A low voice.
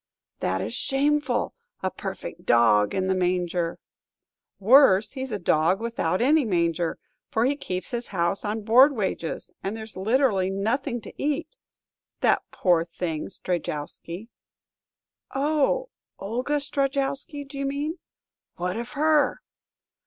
No: high, 220 Hz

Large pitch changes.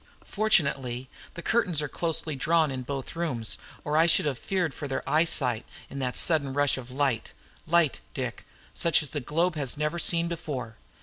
No: average, 4.1 semitones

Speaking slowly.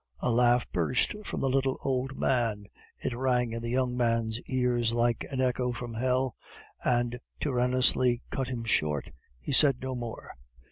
No: average, 160 wpm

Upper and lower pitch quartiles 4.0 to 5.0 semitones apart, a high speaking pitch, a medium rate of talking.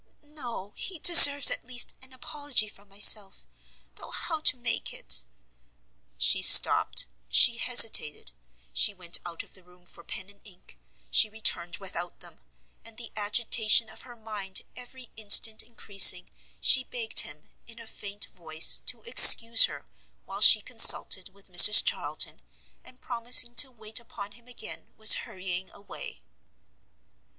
Yes: average, 4.3 semitones; high, 215 Hz; average, 150 wpm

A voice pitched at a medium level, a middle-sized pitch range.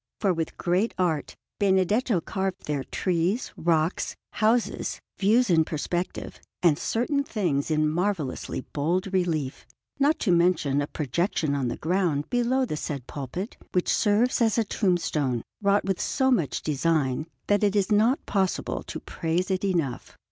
Yes: medium, 180 Hz; average, 5.0 semitones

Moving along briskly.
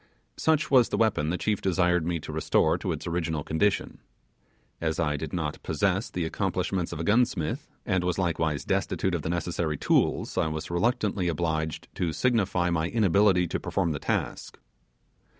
No: average, 170 wpm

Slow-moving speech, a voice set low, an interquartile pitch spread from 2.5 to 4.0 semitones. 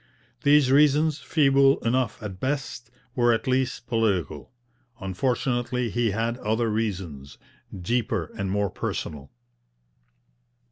No: slow, 105 wpm; low, 120 Hz; average, 4.5 semitones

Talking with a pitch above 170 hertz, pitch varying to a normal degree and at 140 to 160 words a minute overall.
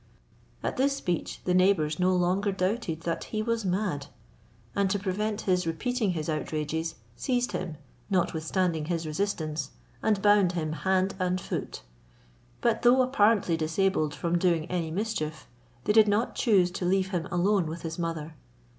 Yes: medium, 185 Hz; average, 4.0 semitones; average, 155 wpm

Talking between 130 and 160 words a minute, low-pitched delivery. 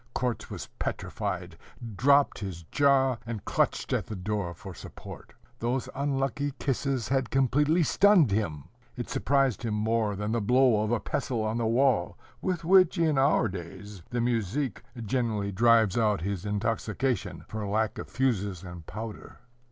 Yes: average, 155 wpm; low, 115 Hz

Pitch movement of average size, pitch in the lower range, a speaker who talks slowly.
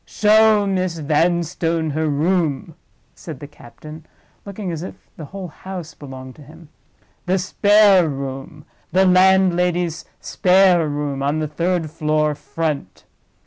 No: average, 3.6 semitones; medium, 165 Hz; slow, 130 wpm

